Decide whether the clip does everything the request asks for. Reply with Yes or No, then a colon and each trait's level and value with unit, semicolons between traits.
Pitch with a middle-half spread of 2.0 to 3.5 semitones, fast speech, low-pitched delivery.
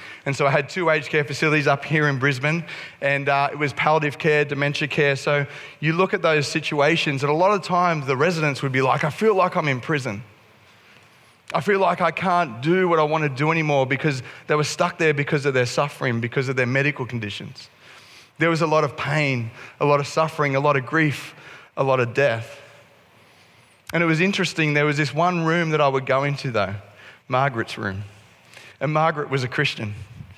No: average, 2.8 semitones; fast, 215 wpm; medium, 145 Hz